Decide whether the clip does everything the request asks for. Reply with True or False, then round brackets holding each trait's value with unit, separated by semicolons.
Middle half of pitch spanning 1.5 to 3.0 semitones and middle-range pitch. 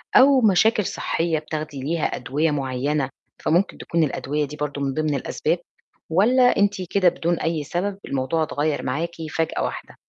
False (3.7 semitones; 160 Hz)